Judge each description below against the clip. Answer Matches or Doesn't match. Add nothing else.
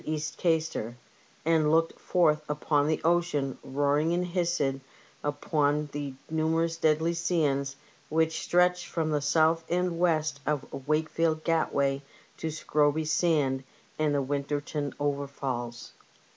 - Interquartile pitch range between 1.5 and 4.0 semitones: Matches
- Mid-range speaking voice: Matches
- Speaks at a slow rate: Matches